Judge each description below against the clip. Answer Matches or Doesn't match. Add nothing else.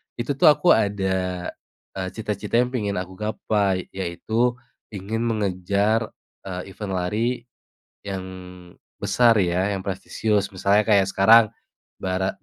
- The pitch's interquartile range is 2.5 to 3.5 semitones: Matches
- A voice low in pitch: Matches